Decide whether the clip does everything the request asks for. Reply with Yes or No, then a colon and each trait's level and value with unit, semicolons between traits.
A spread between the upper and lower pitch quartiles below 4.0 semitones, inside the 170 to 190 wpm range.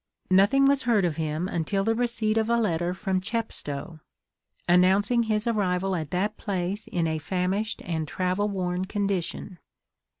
No: average, 3.4 semitones; average, 155 wpm